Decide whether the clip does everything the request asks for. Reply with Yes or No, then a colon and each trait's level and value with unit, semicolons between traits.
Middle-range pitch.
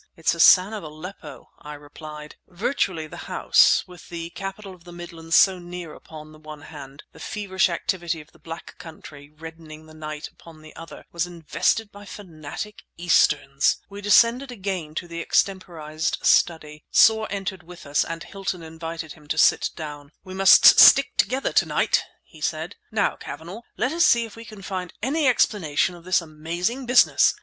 Yes: medium, 170 Hz